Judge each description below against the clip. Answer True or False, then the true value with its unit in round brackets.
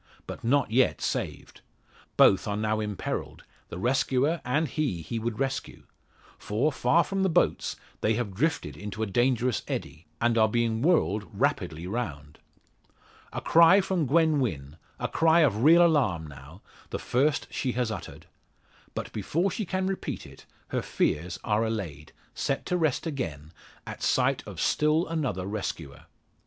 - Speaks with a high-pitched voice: False (120 Hz)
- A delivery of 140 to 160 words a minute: True (155 wpm)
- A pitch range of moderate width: False (7.9 semitones)